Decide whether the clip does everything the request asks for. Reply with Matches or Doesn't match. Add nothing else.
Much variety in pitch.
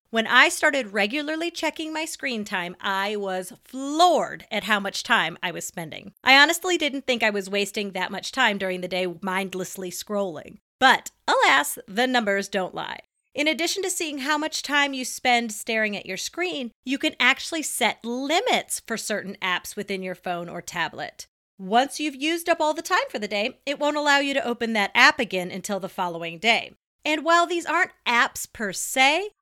Matches